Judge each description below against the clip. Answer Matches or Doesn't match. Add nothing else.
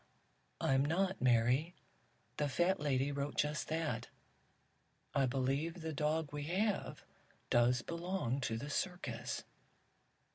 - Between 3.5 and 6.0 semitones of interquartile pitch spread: Matches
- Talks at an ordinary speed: Doesn't match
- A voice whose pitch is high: Doesn't match